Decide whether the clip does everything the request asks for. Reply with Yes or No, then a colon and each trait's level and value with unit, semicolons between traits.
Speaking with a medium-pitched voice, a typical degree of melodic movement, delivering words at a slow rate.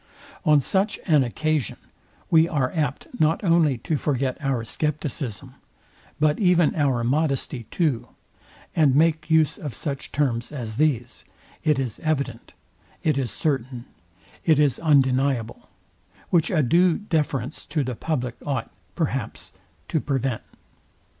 Yes: medium, 145 Hz; average, 3.5 semitones; slow, 130 wpm